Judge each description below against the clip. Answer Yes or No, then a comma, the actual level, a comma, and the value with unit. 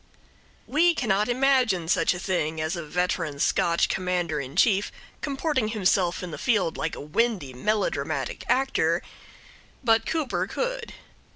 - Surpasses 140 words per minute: No, slow, 135 wpm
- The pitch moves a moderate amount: No, wide, 6.7 semitones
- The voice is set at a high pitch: Yes, high, 195 Hz